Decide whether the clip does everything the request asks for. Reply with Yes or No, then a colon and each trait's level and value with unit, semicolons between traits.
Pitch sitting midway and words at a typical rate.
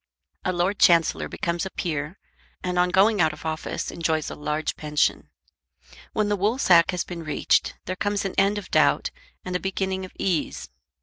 Yes: medium, 180 Hz; average, 180 wpm